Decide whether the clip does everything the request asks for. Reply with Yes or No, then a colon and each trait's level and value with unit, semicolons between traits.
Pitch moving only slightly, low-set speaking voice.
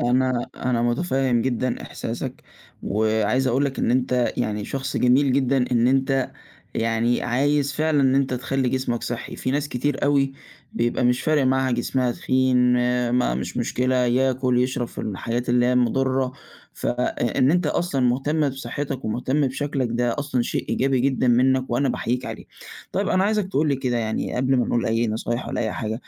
Yes: narrow, 2.0 semitones; low, 130 Hz